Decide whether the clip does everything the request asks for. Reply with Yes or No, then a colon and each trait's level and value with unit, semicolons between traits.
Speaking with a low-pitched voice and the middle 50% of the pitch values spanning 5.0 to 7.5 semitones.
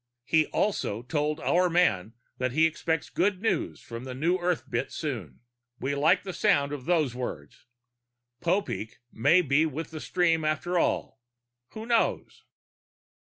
No: medium, 155 Hz; wide, 5.5 semitones